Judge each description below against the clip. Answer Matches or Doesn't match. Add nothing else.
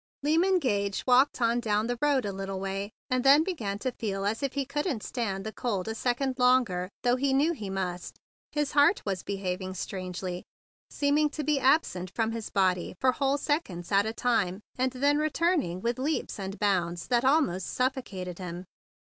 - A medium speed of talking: Matches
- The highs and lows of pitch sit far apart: Matches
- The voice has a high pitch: Matches